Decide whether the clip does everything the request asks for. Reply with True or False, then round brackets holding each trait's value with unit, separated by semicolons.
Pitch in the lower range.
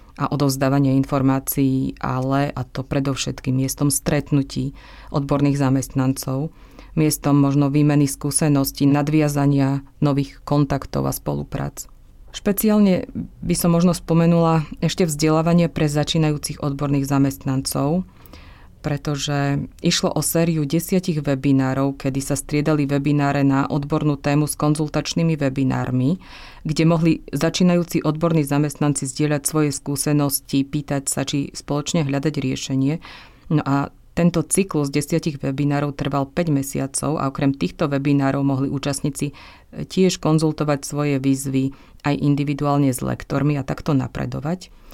False (145 Hz)